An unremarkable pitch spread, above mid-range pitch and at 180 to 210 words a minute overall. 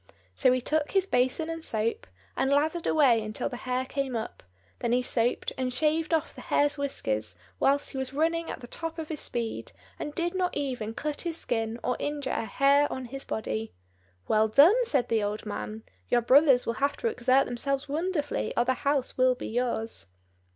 Yes: average, 4.0 semitones; very high, 265 Hz; average, 200 wpm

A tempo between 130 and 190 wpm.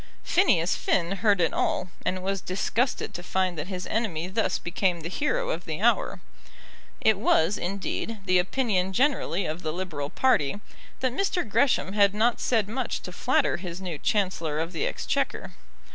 Yes: average, 170 wpm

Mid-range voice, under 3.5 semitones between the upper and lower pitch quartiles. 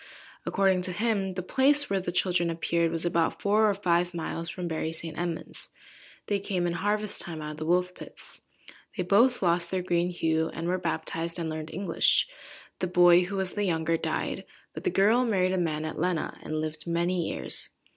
Yes: medium, 175 Hz; narrow, 2.5 semitones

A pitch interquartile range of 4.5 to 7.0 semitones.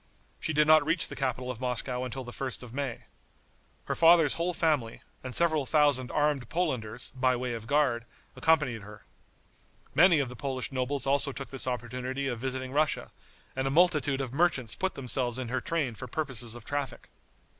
No: average, 3.1 semitones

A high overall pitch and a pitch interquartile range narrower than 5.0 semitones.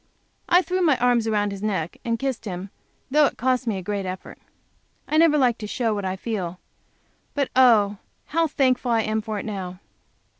Yes: high, 225 Hz; average, 4.5 semitones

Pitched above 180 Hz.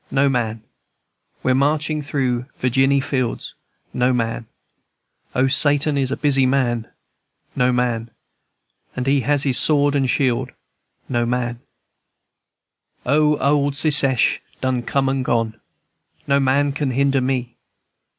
No: low, 135 Hz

